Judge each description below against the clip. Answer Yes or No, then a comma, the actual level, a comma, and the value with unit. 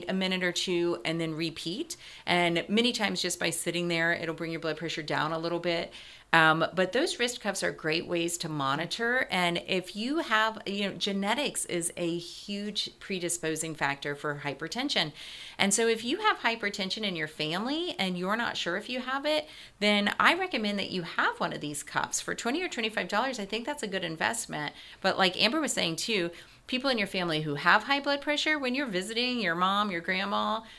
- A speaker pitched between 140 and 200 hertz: Yes, high, 190 Hz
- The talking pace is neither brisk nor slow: No, fast, 210 wpm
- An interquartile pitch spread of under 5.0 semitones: No, average, 5.3 semitones